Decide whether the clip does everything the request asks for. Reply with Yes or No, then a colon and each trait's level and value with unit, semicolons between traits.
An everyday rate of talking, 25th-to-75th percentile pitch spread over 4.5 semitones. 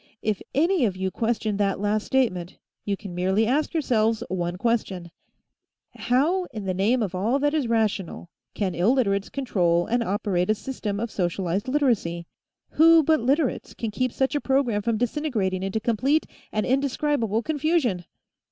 Yes: average, 160 wpm; wide, 5.5 semitones